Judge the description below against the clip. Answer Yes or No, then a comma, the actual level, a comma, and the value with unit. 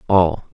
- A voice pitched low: Yes, very low, 85 Hz